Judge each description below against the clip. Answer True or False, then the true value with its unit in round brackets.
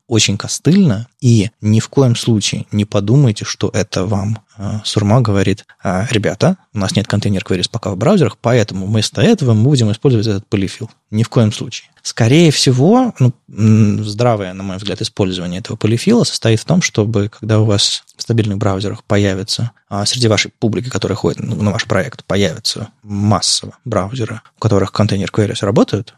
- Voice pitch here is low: True (110 Hz)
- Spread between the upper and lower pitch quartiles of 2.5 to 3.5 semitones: True (2.9 semitones)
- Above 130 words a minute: True (160 wpm)